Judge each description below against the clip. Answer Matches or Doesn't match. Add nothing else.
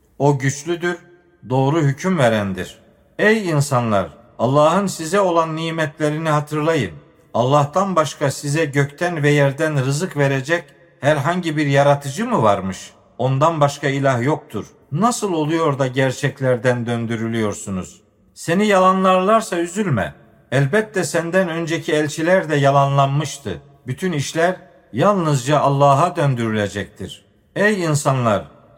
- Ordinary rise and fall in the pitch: Matches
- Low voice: Doesn't match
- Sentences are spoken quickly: Doesn't match